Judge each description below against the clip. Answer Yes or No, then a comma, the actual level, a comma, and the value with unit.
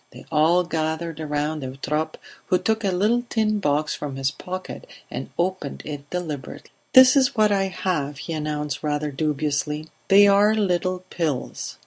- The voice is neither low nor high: Yes, medium, 160 Hz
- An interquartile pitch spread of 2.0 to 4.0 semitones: No, average, 4.5 semitones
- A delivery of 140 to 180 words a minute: Yes, average, 155 wpm